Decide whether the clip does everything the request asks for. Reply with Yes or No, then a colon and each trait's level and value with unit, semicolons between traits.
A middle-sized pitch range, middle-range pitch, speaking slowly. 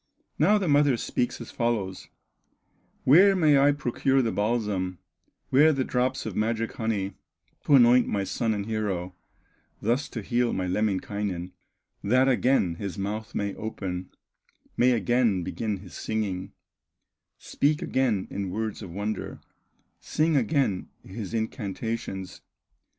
No: average, 4.5 semitones; low, 110 Hz; slow, 130 wpm